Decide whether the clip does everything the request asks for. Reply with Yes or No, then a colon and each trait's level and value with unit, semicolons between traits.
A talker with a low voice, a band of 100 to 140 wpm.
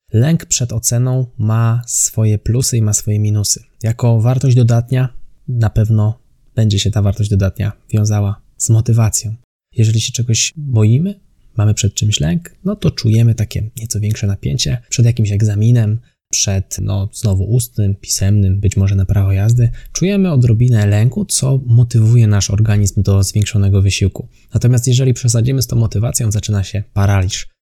No: low, 110 Hz; average, 150 wpm